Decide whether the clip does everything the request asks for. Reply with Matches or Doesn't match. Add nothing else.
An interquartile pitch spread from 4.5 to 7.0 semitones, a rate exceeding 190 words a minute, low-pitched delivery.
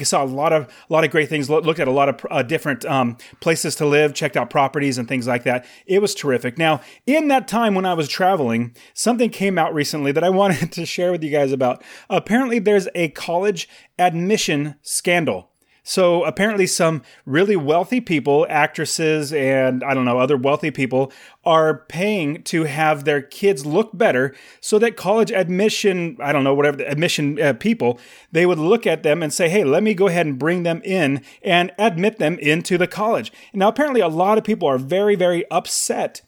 Doesn't match